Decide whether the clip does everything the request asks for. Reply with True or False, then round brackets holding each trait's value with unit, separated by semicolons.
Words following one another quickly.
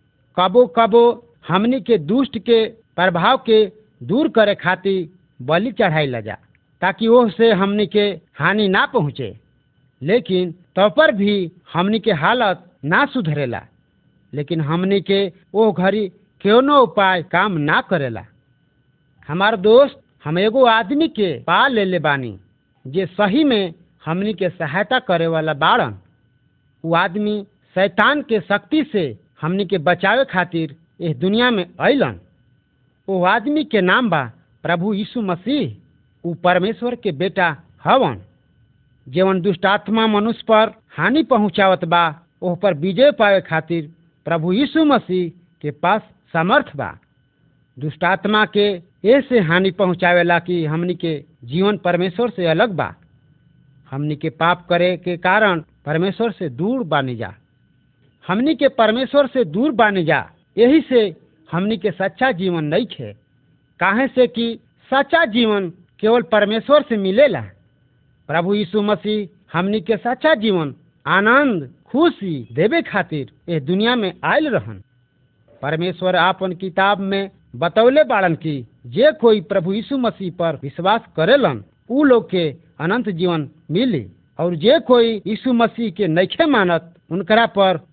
False (140 wpm)